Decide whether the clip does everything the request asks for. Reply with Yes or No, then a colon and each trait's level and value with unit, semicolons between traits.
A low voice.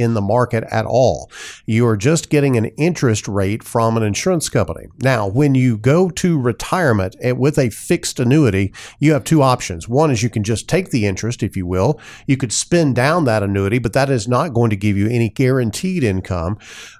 Yes: low, 120 Hz